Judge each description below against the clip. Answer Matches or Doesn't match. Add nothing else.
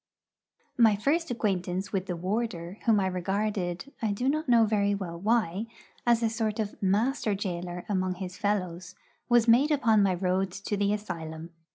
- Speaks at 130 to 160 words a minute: Doesn't match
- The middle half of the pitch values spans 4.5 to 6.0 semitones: Doesn't match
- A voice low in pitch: Doesn't match